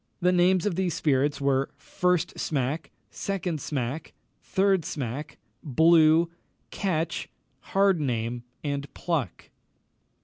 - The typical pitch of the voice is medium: Yes, medium, 160 Hz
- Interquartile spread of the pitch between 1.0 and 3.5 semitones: No, average, 4.4 semitones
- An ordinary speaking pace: No, slow, 100 wpm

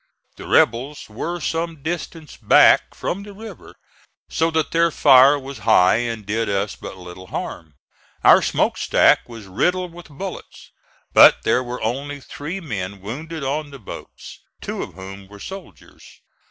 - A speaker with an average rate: Yes, average, 155 wpm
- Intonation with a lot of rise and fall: Yes, wide, 7.6 semitones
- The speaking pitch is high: No, low, 135 Hz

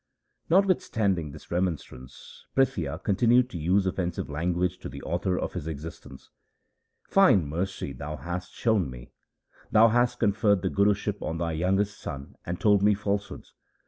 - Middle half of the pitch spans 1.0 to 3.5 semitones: No, average, 4.0 semitones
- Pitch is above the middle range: No, very low, 95 Hz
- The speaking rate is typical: Yes, average, 160 wpm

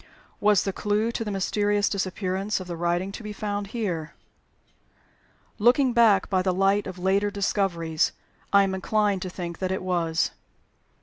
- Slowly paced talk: No, average, 165 wpm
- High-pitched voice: Yes, high, 195 Hz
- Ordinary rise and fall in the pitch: No, narrow, 2.0 semitones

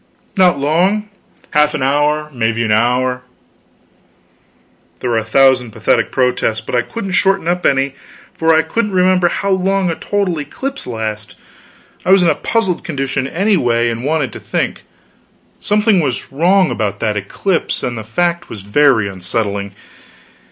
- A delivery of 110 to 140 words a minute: No, average, 155 wpm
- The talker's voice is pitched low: No, medium, 145 Hz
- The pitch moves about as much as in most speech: No, wide, 7.6 semitones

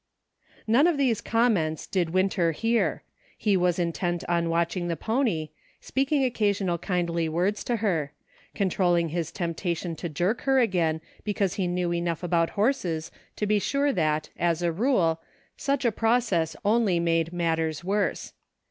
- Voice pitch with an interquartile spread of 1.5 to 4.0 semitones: No, average, 4.5 semitones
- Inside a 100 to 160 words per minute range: Yes, average, 155 wpm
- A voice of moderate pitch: Yes, medium, 180 Hz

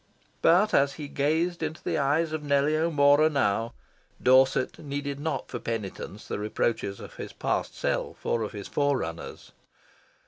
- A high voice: No, medium, 140 Hz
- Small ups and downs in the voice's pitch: No, average, 4.9 semitones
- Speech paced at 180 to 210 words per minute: No, average, 150 wpm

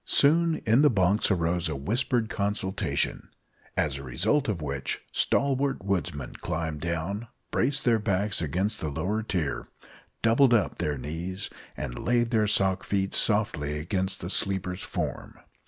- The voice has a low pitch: Yes, very low, 95 Hz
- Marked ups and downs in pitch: Yes, wide, 5.7 semitones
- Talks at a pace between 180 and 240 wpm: No, average, 145 wpm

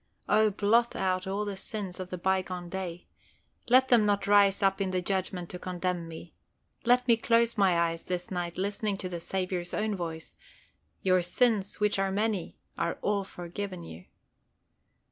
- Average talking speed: Yes, average, 170 wpm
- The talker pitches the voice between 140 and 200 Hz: Yes, high, 190 Hz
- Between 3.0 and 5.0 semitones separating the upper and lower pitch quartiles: No, narrow, 2.6 semitones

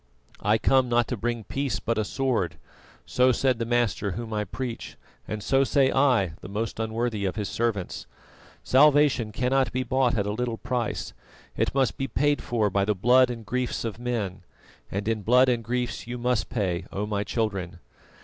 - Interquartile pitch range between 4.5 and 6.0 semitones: No, average, 3.2 semitones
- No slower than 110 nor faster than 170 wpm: No, average, 190 wpm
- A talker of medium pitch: No, low, 120 Hz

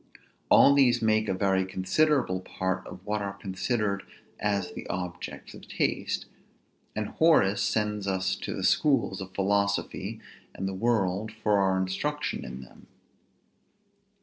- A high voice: No, low, 100 Hz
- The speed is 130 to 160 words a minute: Yes, average, 140 wpm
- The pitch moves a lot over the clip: No, narrow, 2.5 semitones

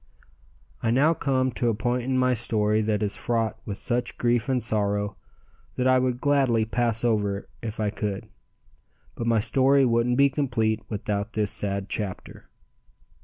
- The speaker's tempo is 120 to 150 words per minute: No, average, 165 wpm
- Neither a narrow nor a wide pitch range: Yes, average, 3.2 semitones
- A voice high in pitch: No, low, 115 Hz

